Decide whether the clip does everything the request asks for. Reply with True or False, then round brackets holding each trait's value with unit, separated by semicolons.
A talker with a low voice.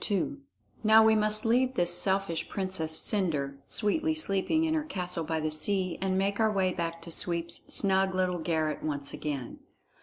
False (185 Hz)